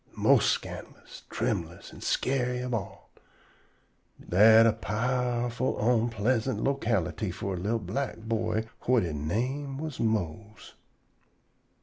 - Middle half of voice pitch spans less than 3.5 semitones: Yes, average, 3.0 semitones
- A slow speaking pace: Yes, slow, 110 wpm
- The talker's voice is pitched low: Yes, low, 115 Hz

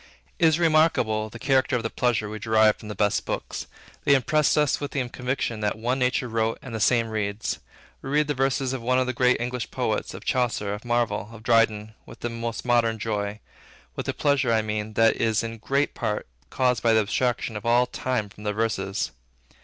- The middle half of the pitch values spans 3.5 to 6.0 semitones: No, average, 2.9 semitones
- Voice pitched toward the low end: Yes, low, 115 Hz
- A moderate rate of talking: No, fast, 215 wpm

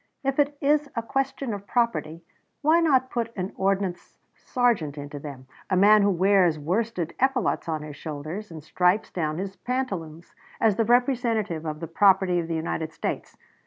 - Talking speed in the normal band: Yes, average, 170 wpm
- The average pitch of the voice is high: Yes, high, 195 Hz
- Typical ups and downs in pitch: No, wide, 6.6 semitones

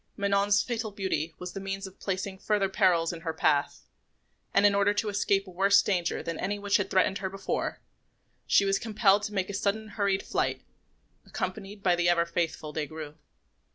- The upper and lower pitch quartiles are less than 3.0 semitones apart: Yes, narrow, 2.4 semitones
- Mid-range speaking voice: No, high, 195 Hz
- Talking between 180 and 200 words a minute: Yes, average, 190 wpm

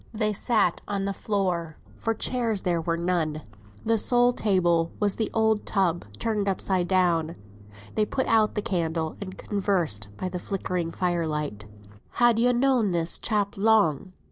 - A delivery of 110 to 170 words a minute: Yes, average, 160 wpm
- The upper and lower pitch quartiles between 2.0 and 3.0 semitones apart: No, average, 4.3 semitones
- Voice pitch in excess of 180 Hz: Yes, high, 190 Hz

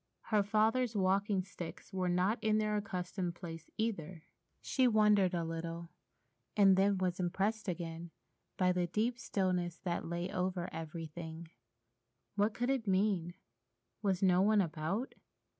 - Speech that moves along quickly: No, average, 140 wpm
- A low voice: No, medium, 185 Hz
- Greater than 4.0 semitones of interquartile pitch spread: No, average, 3.5 semitones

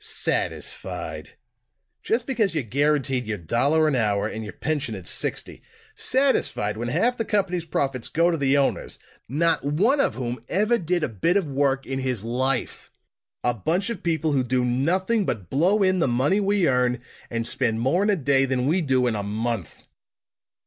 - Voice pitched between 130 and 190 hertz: Yes, medium, 140 Hz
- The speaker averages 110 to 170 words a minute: No, average, 185 wpm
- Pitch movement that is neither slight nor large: No, wide, 6.6 semitones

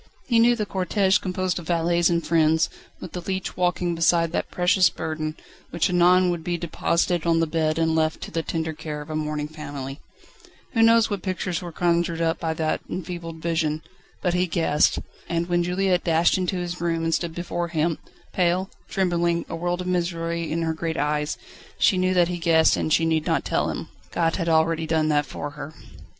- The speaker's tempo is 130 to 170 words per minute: No, fast, 205 wpm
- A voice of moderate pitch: Yes, medium, 170 Hz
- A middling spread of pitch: No, narrow, 1.8 semitones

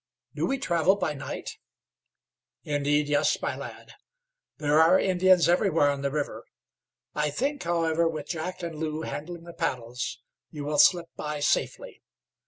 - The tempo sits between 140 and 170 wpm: Yes, average, 150 wpm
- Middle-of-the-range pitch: Yes, medium, 160 Hz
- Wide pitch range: No, average, 2.8 semitones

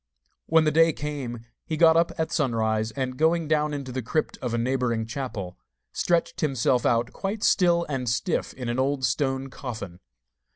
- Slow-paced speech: No, average, 175 wpm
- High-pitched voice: No, low, 135 Hz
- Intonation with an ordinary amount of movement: Yes, average, 4.8 semitones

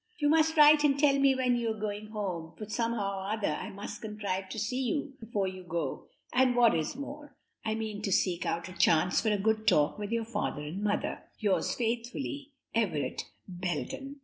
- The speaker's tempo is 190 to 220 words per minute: Yes, average, 200 wpm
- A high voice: Yes, high, 215 Hz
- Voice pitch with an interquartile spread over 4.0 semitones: Yes, average, 4.9 semitones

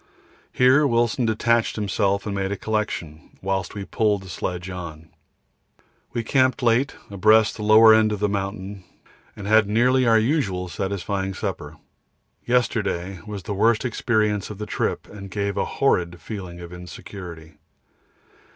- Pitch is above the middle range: No, low, 100 Hz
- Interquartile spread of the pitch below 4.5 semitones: Yes, average, 2.8 semitones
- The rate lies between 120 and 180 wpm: Yes, average, 150 wpm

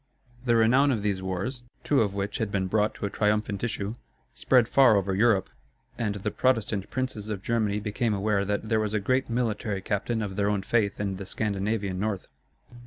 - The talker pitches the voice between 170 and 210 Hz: No, low, 105 Hz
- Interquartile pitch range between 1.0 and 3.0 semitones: Yes, narrow, 2.4 semitones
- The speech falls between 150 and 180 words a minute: No, average, 195 wpm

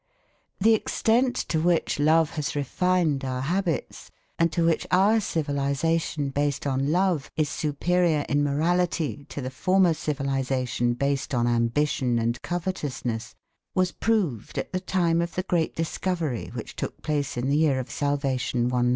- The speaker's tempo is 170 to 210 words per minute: No, average, 150 wpm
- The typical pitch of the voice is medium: Yes, medium, 150 Hz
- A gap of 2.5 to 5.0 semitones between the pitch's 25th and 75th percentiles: Yes, average, 4.5 semitones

